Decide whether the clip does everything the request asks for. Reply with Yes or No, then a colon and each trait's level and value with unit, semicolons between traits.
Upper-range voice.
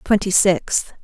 Yes: high, 195 Hz